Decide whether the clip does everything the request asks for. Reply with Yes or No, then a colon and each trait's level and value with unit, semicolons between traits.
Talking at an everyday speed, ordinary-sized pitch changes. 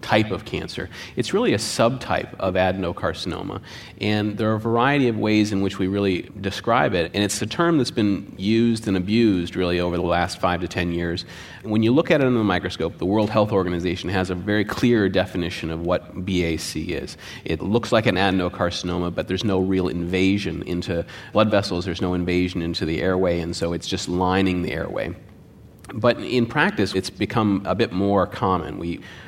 Yes: average, 195 wpm; average, 3.2 semitones